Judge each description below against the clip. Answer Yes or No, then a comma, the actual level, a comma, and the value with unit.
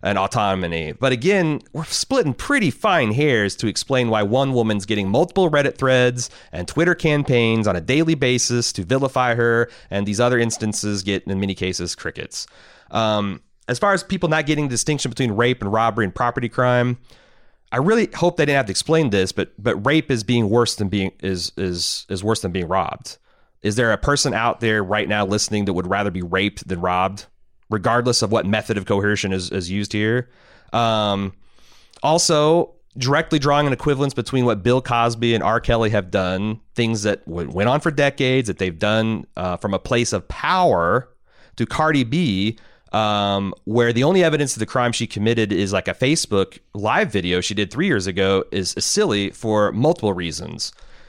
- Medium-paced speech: Yes, average, 190 wpm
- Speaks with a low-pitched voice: Yes, low, 115 Hz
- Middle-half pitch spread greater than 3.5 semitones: Yes, average, 4.6 semitones